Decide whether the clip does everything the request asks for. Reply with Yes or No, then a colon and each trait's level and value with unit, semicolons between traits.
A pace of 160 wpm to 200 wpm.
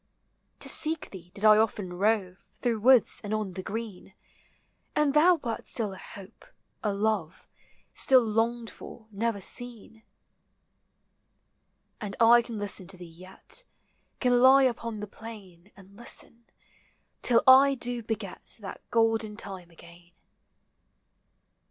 No: slow, 135 wpm